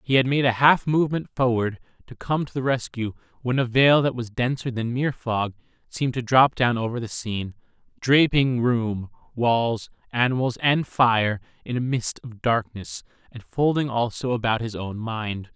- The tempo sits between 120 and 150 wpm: No, average, 175 wpm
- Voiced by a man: Yes, male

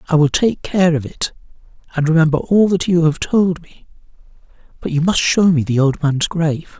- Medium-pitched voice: Yes, medium, 165 Hz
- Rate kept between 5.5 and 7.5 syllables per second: No, 5.1 syllables/s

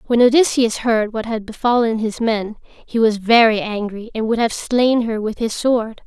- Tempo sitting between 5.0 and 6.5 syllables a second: No, 4.5 syllables/s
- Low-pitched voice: No, high, 225 Hz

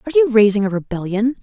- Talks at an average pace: No, fast, 210 wpm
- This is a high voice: Yes, high, 205 Hz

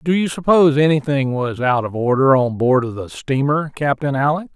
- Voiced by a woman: No, male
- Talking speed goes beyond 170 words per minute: Yes, average, 200 wpm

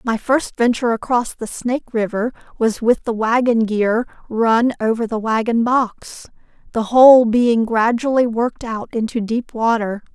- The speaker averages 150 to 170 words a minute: Yes, average, 155 wpm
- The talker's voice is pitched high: Yes, high, 230 Hz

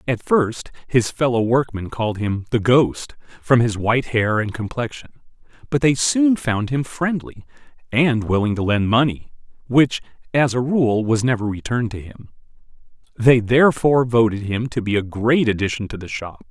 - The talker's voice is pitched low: Yes, low, 120 Hz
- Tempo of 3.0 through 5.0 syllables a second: Yes, 4.9 syllables/s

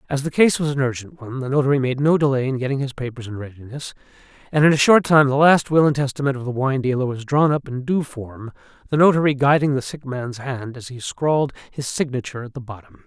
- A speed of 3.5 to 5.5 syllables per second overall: No, 6.2 syllables/s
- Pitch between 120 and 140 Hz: Yes, low, 135 Hz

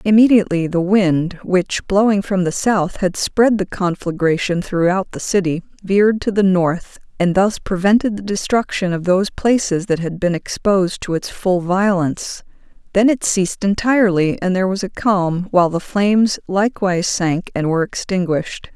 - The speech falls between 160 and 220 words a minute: Yes, average, 165 wpm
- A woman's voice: Yes, female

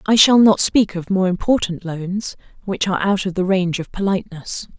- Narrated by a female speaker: Yes, female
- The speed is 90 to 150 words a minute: No, average, 200 wpm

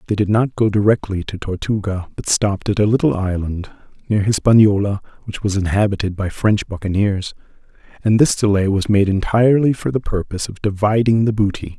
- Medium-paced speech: Yes, average, 175 wpm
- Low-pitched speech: Yes, low, 105 Hz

